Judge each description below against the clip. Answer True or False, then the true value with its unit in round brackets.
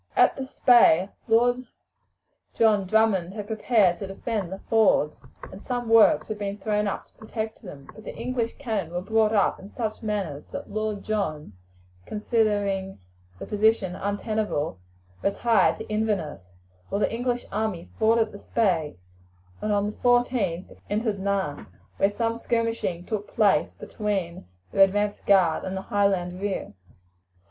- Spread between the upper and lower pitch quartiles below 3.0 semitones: True (2.6 semitones)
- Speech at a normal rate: True (150 wpm)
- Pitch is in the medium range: False (205 Hz)